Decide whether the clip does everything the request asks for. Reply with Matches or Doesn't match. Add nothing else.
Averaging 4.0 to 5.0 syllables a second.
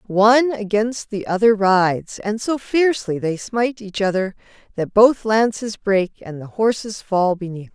Matches